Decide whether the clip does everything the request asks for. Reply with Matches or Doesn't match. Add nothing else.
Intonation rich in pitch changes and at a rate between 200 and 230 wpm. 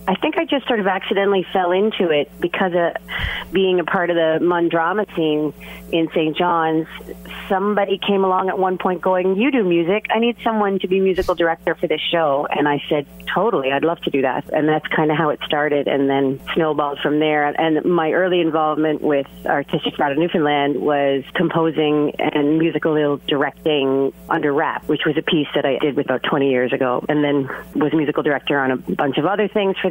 Doesn't match